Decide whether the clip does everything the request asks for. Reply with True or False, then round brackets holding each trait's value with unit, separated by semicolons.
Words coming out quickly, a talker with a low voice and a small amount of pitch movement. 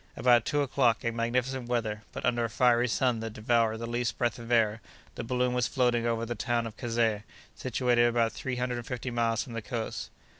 True (215 wpm; 120 Hz; 1.4 semitones)